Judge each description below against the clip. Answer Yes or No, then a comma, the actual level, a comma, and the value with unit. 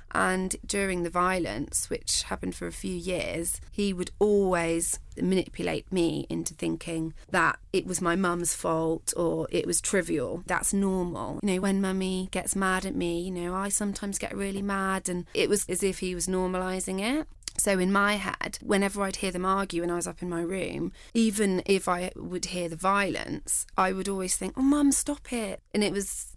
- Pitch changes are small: Yes, narrow, 2.2 semitones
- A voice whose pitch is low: No, medium, 185 Hz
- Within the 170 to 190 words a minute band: No, average, 200 wpm